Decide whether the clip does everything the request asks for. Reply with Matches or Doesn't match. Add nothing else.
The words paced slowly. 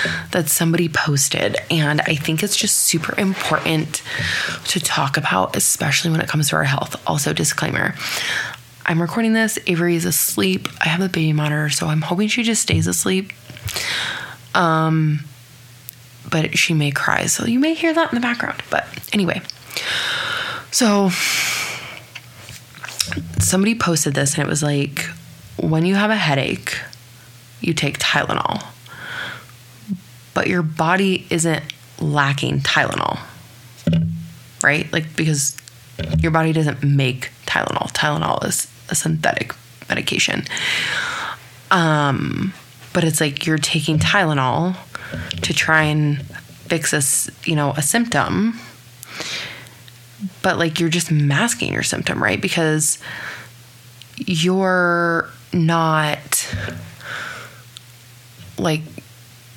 Matches